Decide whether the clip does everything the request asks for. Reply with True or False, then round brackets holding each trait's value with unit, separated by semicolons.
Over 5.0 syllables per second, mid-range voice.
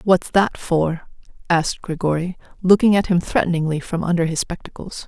True (5.3 syllables/s; 175 Hz)